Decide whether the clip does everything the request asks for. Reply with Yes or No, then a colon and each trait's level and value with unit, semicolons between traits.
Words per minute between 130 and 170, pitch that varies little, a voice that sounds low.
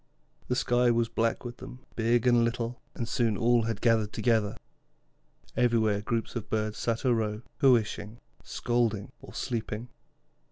Yes: average, 150 wpm; narrow, 1.7 semitones; low, 115 Hz